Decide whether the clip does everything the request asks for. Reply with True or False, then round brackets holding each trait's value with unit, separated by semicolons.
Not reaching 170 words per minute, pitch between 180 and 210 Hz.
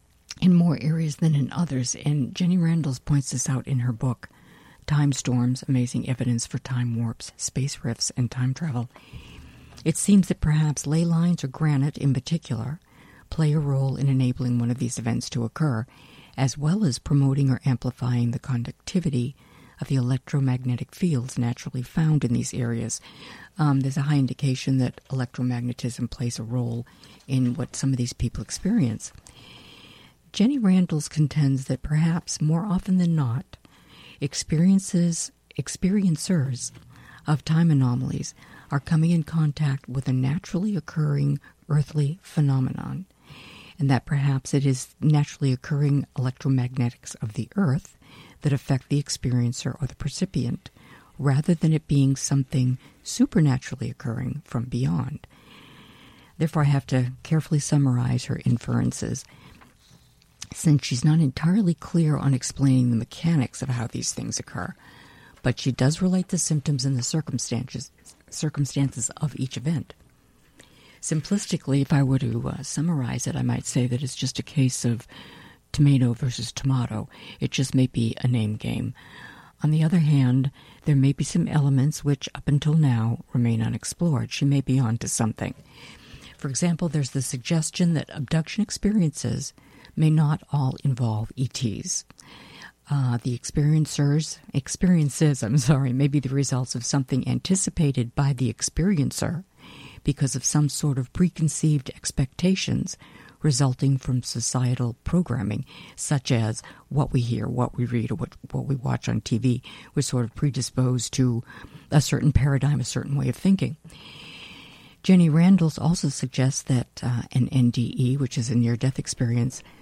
False (150 wpm; 135 Hz)